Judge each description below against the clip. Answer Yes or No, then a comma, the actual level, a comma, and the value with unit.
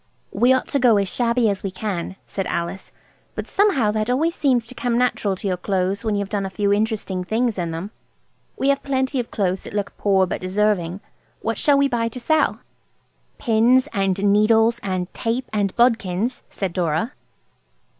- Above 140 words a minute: Yes, average, 185 wpm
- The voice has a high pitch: Yes, high, 210 Hz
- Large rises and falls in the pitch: No, average, 4.2 semitones